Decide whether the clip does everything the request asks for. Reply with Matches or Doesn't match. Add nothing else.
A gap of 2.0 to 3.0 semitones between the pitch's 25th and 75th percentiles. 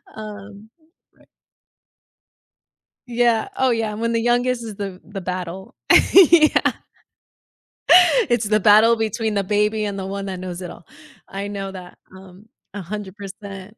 Matches